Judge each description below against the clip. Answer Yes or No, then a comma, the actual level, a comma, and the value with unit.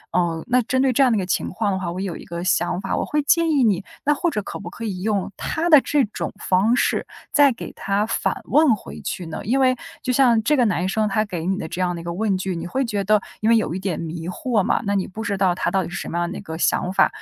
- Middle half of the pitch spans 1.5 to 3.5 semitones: No, average, 5.1 semitones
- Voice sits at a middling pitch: No, high, 200 Hz